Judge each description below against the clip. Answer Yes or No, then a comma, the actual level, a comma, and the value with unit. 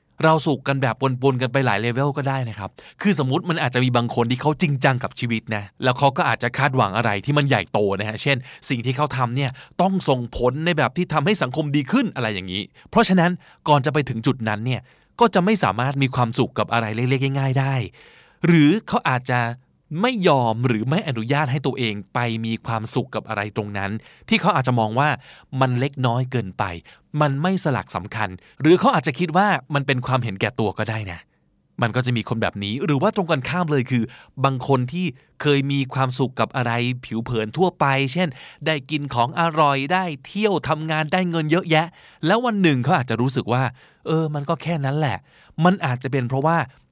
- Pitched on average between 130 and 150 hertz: Yes, low, 135 Hz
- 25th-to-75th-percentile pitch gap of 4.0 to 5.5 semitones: Yes, average, 4.8 semitones